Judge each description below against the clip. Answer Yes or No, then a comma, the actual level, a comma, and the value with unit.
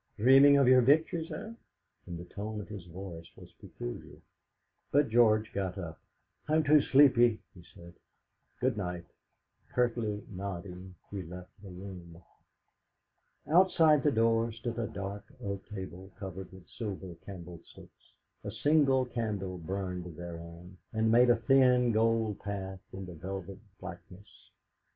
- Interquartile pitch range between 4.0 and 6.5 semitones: Yes, average, 4.7 semitones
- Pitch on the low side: Yes, low, 100 Hz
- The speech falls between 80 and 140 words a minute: Yes, slow, 135 wpm